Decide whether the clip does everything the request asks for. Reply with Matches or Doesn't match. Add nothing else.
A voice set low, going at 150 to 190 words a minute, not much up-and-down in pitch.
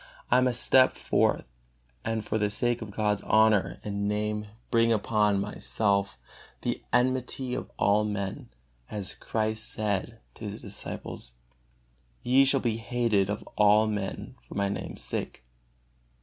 Doesn't match